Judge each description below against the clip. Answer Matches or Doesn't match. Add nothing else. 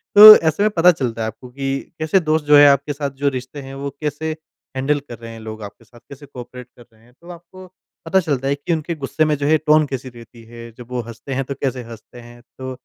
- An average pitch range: Matches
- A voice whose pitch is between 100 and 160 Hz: Matches